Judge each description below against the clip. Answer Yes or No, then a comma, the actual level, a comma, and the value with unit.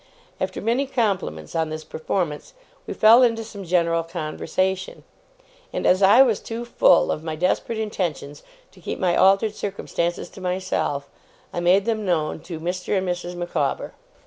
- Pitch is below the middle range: No, medium, 180 Hz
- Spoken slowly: No, average, 160 wpm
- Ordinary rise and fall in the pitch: Yes, average, 3.8 semitones